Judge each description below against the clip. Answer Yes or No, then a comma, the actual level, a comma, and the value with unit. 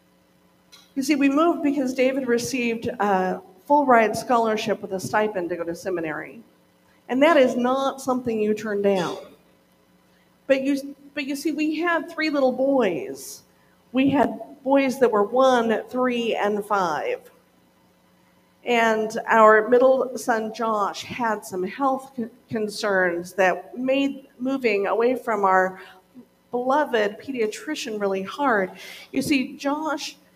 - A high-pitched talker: Yes, high, 235 Hz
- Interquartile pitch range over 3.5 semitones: Yes, average, 5.1 semitones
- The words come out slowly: Yes, slow, 130 wpm